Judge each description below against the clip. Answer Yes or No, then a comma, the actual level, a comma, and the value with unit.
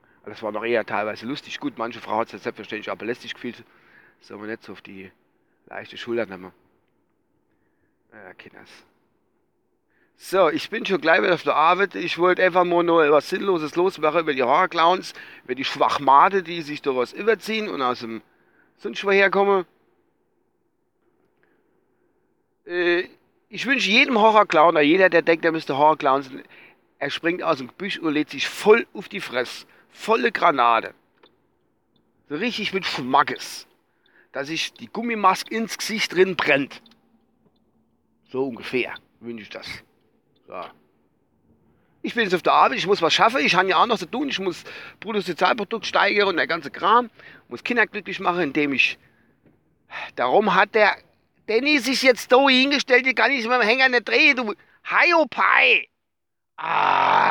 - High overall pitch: Yes, high, 195 Hz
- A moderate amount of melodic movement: No, wide, 8.6 semitones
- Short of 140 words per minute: No, average, 165 wpm